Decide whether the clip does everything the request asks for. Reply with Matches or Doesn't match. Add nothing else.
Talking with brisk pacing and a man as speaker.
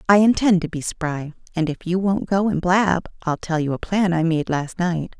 Doesn't match